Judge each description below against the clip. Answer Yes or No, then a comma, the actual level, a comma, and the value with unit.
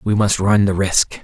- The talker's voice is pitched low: Yes, low, 100 Hz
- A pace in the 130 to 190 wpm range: No, fast, 245 wpm